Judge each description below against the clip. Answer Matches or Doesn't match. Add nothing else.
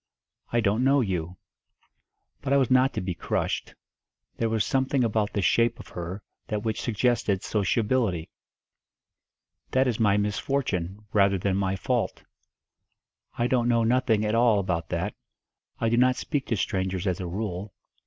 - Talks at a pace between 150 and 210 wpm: Matches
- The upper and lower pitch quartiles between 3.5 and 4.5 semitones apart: Matches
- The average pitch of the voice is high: Doesn't match